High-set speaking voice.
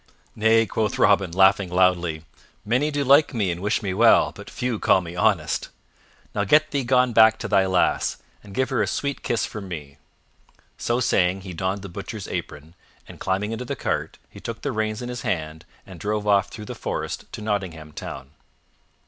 No: low, 100 Hz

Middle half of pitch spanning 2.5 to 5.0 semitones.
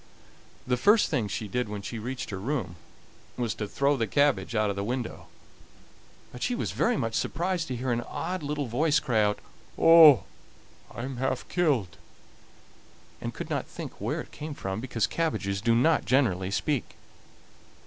No: wide, 5.5 semitones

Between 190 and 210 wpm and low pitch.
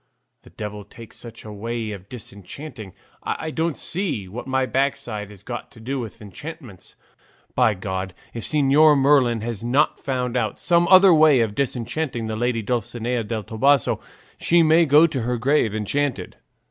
No: average, 165 wpm; low, 120 Hz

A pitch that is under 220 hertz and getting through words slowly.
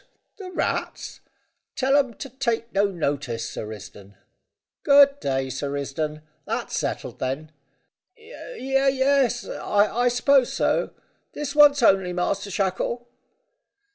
No: high, 230 Hz; slow, 115 wpm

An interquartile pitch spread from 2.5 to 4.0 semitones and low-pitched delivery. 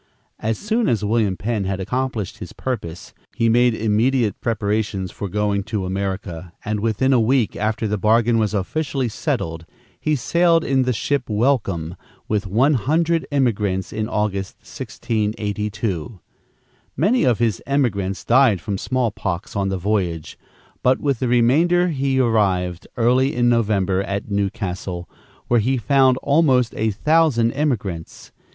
No: average, 4.7 semitones; low, 110 Hz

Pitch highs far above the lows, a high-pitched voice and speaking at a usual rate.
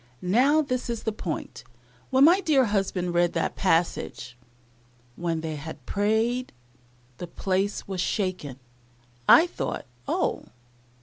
No: wide, 6.4 semitones; high, 195 Hz; slow, 125 wpm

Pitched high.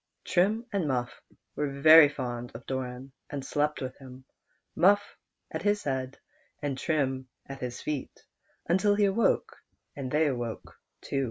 No: medium, 140 Hz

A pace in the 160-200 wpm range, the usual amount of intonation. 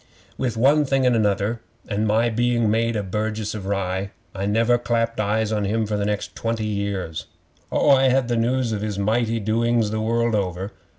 No: average, 195 wpm; narrow, 2.3 semitones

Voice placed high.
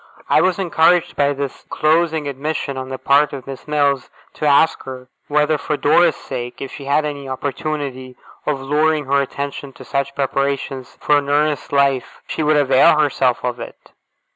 No: medium, 140 Hz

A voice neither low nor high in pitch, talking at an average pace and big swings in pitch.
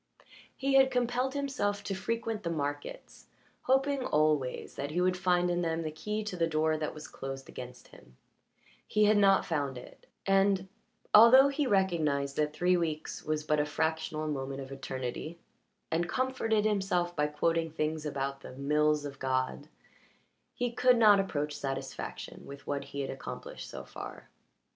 Yes: medium, 160 Hz; average, 165 wpm; wide, 6.0 semitones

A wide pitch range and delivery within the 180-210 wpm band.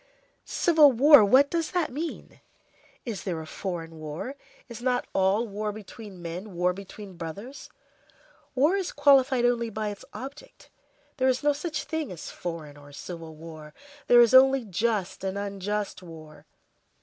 No: wide, 6.9 semitones; average, 150 wpm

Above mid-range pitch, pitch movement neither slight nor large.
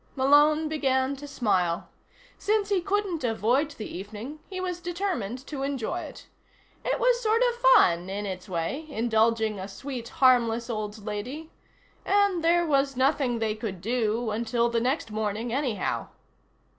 No: very high, 250 Hz; wide, 6.2 semitones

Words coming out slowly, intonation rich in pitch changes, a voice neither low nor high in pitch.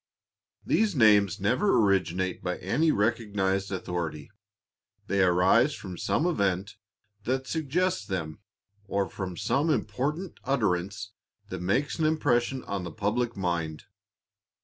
No: slow, 120 wpm; wide, 6.3 semitones; low, 100 Hz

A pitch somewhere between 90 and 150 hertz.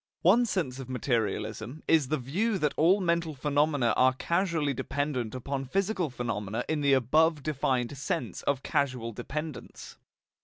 Yes: medium, 140 Hz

